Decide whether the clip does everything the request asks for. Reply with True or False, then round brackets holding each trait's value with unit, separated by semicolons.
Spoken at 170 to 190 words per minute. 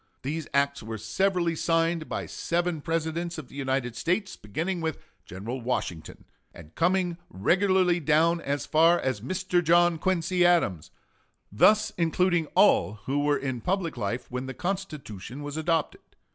False (145 wpm)